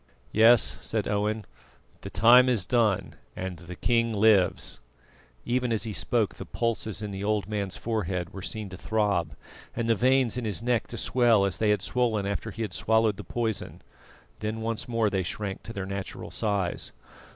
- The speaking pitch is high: No, low, 110 Hz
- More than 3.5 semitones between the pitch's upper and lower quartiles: No, average, 2.7 semitones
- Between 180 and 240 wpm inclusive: Yes, average, 185 wpm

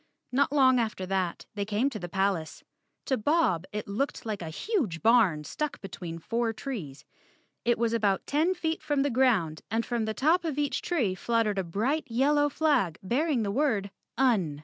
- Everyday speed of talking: Yes, average, 185 wpm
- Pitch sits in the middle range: No, high, 230 Hz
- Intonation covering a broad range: Yes, wide, 6.3 semitones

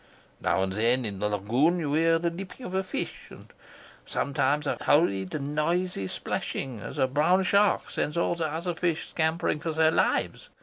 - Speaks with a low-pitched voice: No, medium, 155 Hz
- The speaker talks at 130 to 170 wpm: No, average, 180 wpm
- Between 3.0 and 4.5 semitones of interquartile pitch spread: No, average, 5.0 semitones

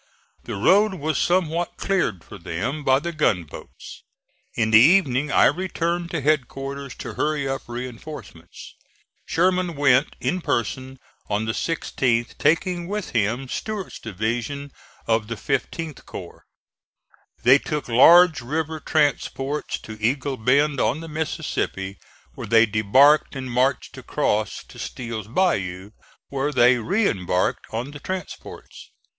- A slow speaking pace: Yes, slow, 130 wpm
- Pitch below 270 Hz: Yes, low, 135 Hz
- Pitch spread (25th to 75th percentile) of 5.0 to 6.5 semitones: Yes, wide, 5.6 semitones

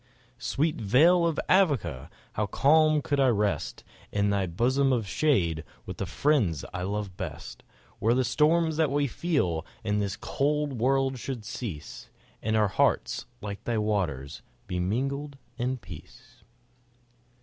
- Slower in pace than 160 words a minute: Yes, average, 145 wpm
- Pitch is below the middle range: Yes, low, 120 Hz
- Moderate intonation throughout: No, wide, 6.1 semitones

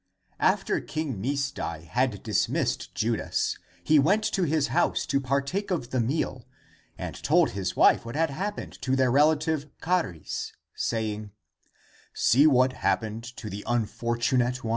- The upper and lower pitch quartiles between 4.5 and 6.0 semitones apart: Yes, average, 5.1 semitones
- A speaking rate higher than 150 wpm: No, average, 145 wpm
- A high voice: No, low, 130 Hz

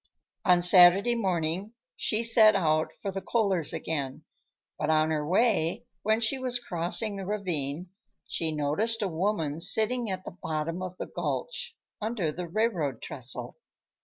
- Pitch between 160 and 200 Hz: Yes, medium, 185 Hz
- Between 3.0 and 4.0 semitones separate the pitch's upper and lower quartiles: No, wide, 5.4 semitones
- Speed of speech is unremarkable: Yes, average, 150 wpm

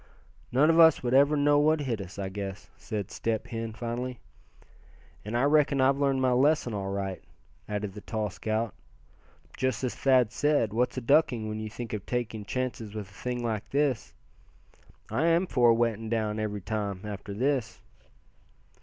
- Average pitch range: Yes, average, 3.9 semitones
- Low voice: Yes, low, 115 Hz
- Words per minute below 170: No, average, 180 wpm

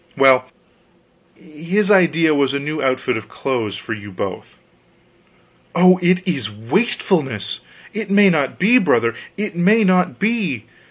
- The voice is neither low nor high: Yes, medium, 155 Hz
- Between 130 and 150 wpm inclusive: Yes, average, 145 wpm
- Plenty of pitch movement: Yes, wide, 7.0 semitones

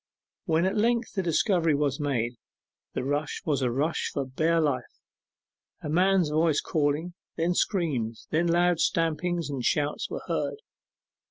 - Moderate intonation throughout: Yes, average, 3.3 semitones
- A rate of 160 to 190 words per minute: No, average, 150 wpm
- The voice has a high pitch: No, medium, 160 Hz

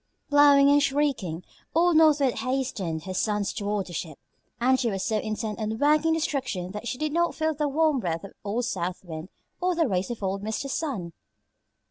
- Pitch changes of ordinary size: No, wide, 7.0 semitones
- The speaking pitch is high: Yes, high, 240 Hz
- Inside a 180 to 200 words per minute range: Yes, average, 195 wpm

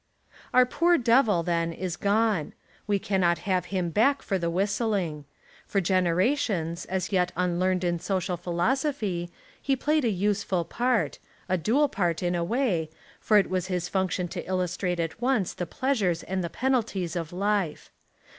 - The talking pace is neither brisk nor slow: Yes, average, 165 wpm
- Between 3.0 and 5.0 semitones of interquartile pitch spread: Yes, average, 4.0 semitones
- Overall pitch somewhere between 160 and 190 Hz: Yes, medium, 185 Hz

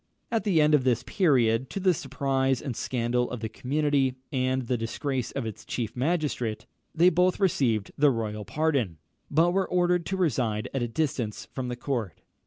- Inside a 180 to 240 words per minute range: Yes, average, 185 wpm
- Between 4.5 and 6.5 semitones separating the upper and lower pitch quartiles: Yes, average, 4.9 semitones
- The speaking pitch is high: No, low, 130 Hz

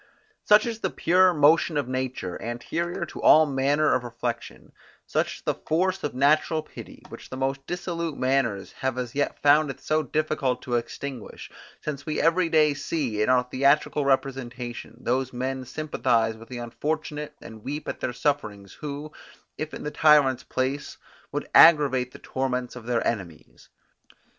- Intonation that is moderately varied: Yes, average, 3.6 semitones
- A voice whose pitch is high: No, low, 135 Hz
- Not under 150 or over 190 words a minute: Yes, average, 165 wpm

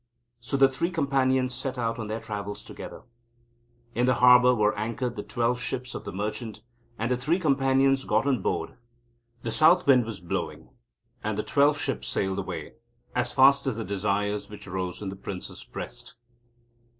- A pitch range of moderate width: Yes, average, 4.2 semitones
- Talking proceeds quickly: No, average, 175 wpm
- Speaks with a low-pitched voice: Yes, low, 120 Hz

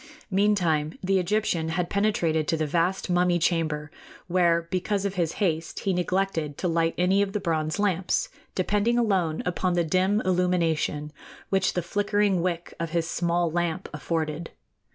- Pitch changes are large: No, average, 2.7 semitones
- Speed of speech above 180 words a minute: No, average, 155 wpm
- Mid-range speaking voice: Yes, medium, 175 Hz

